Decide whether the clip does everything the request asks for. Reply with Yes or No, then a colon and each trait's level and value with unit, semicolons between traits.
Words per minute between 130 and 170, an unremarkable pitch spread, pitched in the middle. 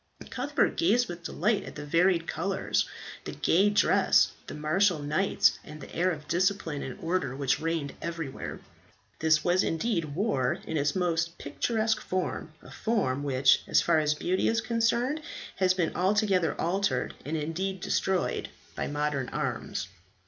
Yes: average, 155 wpm; average, 4.5 semitones; medium, 170 Hz